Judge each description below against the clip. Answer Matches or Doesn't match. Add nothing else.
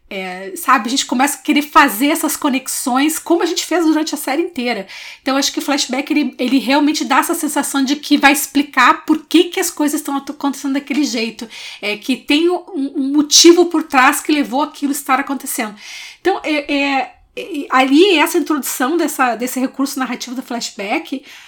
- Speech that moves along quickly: Matches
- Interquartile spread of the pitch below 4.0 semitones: Matches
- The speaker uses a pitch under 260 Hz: Doesn't match